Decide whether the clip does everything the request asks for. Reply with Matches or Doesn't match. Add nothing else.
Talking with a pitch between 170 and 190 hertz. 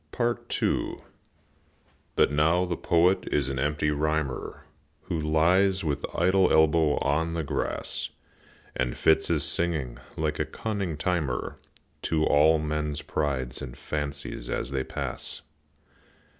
Doesn't match